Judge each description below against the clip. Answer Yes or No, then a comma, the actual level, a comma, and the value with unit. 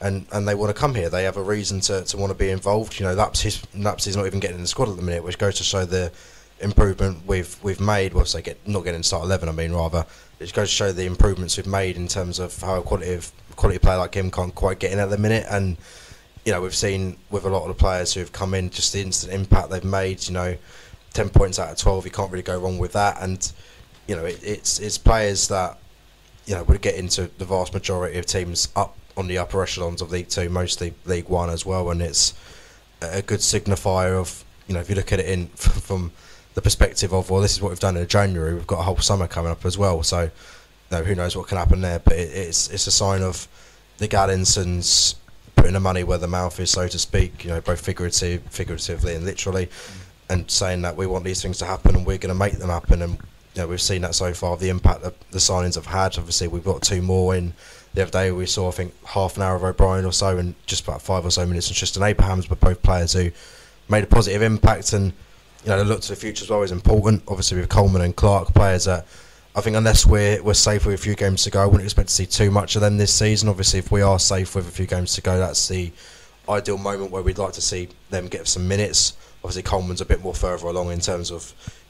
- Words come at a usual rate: No, fast, 260 wpm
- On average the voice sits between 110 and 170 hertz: No, very low, 95 Hz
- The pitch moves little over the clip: Yes, narrow, 1.8 semitones